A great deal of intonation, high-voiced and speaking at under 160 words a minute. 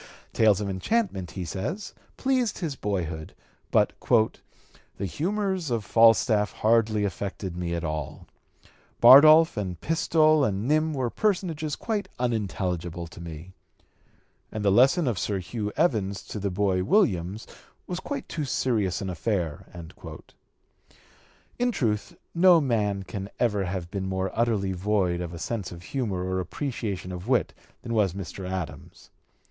No: wide, 6.7 semitones; low, 105 Hz; average, 145 wpm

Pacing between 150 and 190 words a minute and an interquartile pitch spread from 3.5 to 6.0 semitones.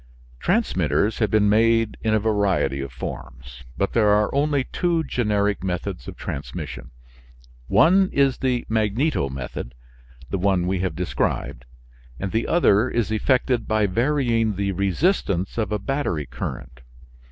No: average, 140 wpm; average, 4.5 semitones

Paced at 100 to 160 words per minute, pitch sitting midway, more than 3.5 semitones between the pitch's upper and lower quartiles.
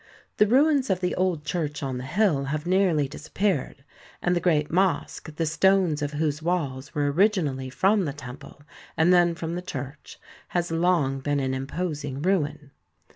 No: average, 170 wpm; medium, 160 Hz; average, 4.2 semitones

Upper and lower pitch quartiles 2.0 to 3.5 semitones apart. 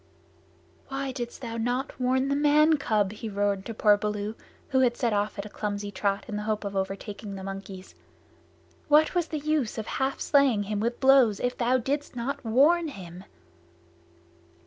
No: average, 4.9 semitones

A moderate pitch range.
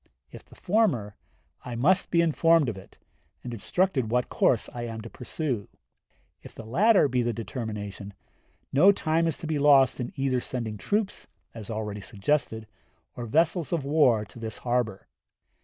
No: wide, 6.1 semitones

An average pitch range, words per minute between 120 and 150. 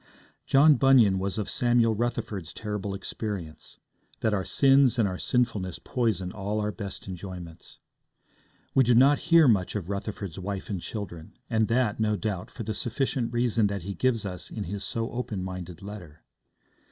No: average, 3.9 semitones; average, 165 wpm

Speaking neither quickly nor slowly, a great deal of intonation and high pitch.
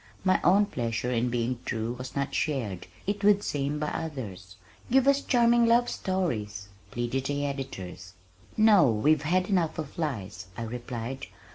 No: average, 155 wpm; wide, 8.1 semitones; medium, 140 Hz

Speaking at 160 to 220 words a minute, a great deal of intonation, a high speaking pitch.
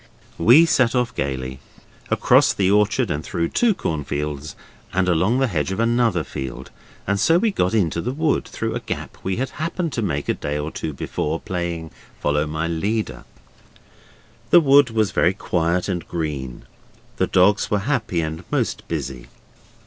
No: average, 170 wpm; wide, 7.0 semitones; very low, 90 Hz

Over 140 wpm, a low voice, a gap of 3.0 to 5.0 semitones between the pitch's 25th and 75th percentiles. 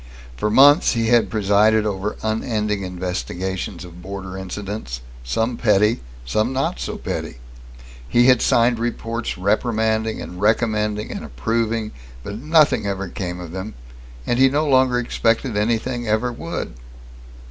No: slow, 135 wpm; low, 110 Hz; average, 3.4 semitones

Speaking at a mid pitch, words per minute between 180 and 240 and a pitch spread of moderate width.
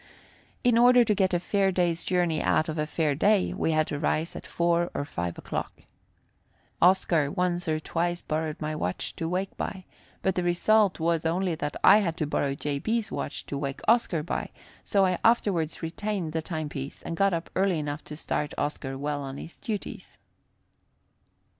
Yes: medium, 170 Hz; average, 185 wpm; average, 3.8 semitones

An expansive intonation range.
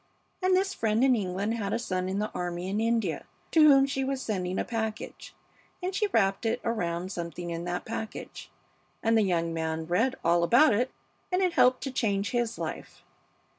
Yes: wide, 5.8 semitones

